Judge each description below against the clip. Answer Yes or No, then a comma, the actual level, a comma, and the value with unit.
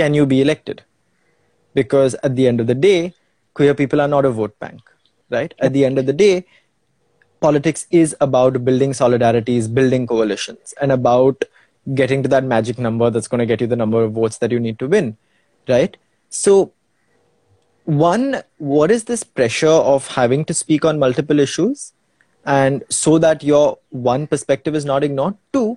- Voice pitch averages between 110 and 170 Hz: Yes, low, 135 Hz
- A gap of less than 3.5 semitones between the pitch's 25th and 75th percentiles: No, average, 4.1 semitones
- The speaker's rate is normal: Yes, average, 180 wpm